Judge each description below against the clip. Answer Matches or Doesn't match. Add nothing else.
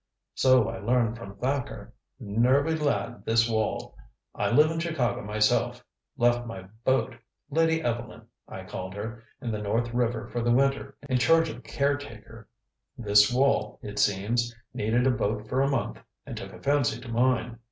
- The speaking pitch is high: Doesn't match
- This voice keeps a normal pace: Matches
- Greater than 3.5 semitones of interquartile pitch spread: Doesn't match